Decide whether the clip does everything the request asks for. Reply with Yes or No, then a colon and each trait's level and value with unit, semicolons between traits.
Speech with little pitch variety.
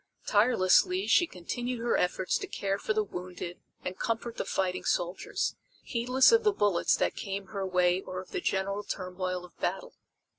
No: average, 4.2 semitones